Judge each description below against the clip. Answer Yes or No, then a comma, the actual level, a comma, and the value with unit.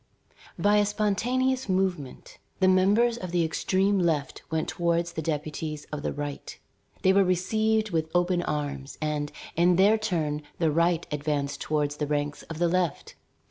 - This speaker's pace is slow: No, average, 160 wpm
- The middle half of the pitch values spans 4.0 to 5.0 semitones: Yes, average, 4.3 semitones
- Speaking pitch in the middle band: Yes, medium, 170 Hz